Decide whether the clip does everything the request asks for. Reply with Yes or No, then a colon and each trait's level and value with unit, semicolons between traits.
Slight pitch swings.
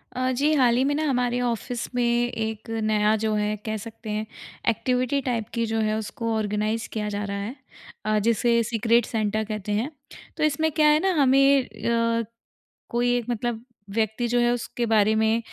Yes: narrow, 2.2 semitones